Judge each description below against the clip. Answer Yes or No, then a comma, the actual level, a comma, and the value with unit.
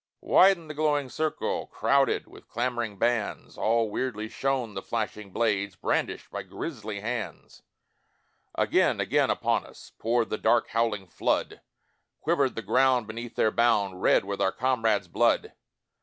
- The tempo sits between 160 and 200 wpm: No, average, 140 wpm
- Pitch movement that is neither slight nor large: Yes, average, 3.6 semitones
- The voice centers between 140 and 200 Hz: No, low, 115 Hz